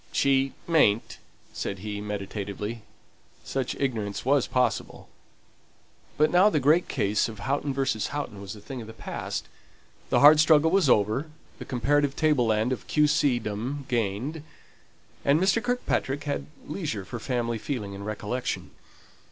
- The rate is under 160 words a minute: Yes, average, 150 wpm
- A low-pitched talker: Yes, low, 130 Hz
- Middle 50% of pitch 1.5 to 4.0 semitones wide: No, wide, 5.5 semitones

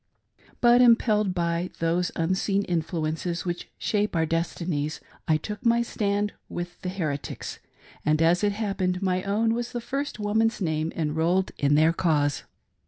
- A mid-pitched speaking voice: Yes, medium, 180 Hz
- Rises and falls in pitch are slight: No, average, 4.2 semitones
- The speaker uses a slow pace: No, average, 165 wpm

